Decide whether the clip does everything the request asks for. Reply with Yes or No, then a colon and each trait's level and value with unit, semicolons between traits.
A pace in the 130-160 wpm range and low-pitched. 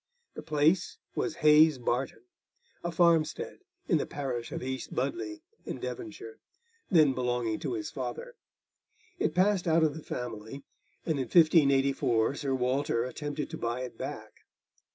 No: average, 145 wpm; medium, 145 Hz